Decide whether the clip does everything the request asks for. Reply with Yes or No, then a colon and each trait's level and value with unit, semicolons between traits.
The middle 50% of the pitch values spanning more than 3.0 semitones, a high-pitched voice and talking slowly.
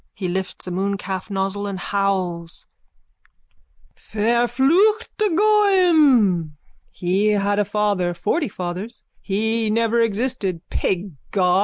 Yes: average, 4.1 semitones; high, 205 Hz; slow, 105 wpm